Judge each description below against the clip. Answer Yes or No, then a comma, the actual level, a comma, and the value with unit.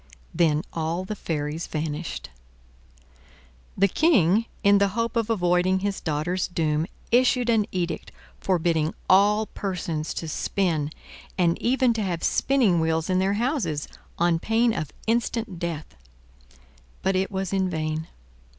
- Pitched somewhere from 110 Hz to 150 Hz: No, medium, 185 Hz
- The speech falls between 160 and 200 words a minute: No, slow, 135 wpm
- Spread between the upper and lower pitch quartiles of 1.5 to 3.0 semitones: No, average, 4.6 semitones